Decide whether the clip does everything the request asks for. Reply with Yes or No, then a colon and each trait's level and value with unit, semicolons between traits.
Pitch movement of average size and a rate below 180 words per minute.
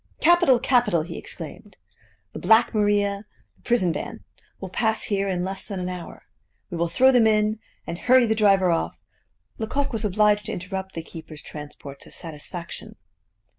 Yes: average, 4.0 semitones; average, 170 wpm